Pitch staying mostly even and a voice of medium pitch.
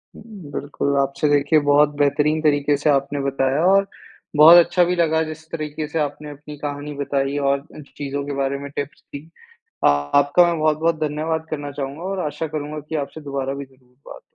Yes: narrow, 1.8 semitones; medium, 145 Hz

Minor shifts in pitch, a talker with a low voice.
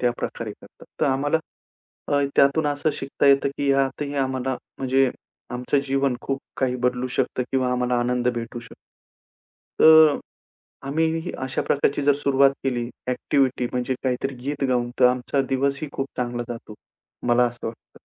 Yes: narrow, 2.0 semitones; low, 130 Hz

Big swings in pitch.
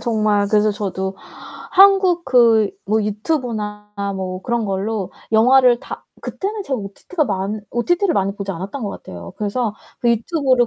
No: average, 4.2 semitones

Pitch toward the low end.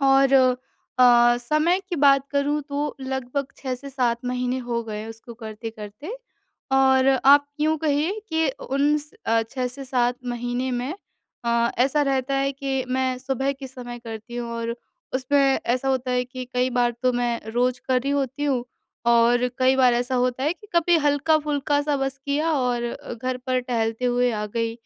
No: very high, 255 Hz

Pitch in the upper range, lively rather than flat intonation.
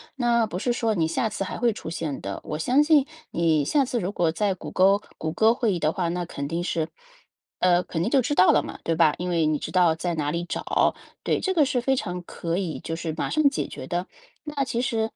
No: medium, 180 Hz; wide, 6.3 semitones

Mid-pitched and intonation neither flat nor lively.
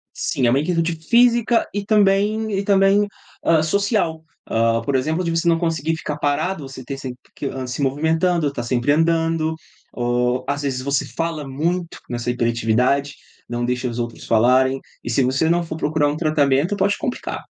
Yes: medium, 150 Hz; average, 4.8 semitones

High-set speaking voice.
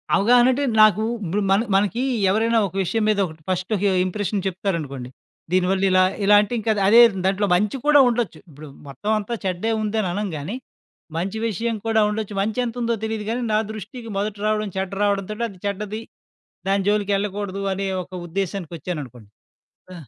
Yes: high, 205 Hz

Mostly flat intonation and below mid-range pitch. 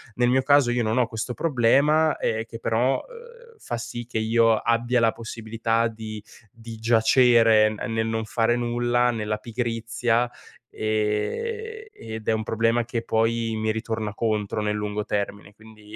Yes: narrow, 1.7 semitones; low, 115 Hz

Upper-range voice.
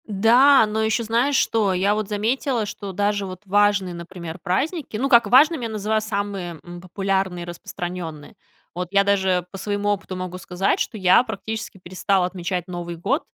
Yes: high, 200 Hz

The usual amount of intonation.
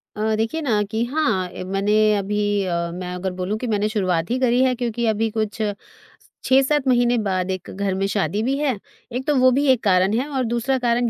Yes: average, 4.2 semitones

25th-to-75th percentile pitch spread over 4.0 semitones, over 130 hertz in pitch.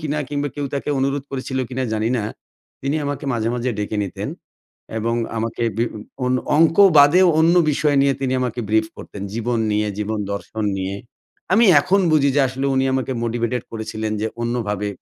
No: average, 4.4 semitones; low, 125 Hz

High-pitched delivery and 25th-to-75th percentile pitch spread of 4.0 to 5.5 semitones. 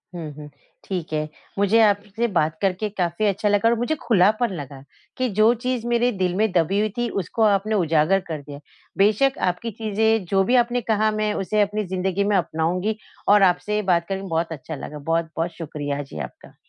Yes: high, 195 Hz; average, 4.5 semitones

